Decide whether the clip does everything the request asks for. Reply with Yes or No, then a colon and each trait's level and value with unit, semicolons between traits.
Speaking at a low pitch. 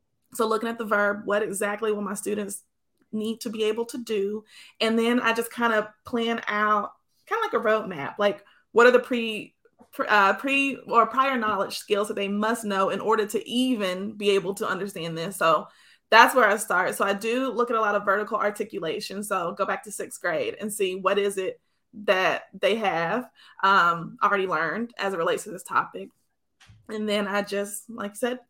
No: high, 215 Hz